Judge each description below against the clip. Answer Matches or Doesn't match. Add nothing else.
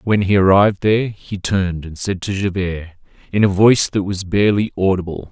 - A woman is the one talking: Doesn't match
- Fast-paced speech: Doesn't match